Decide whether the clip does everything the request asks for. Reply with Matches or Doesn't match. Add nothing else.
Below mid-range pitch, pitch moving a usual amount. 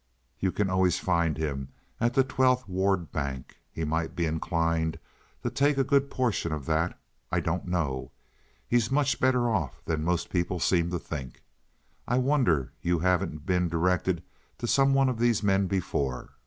Doesn't match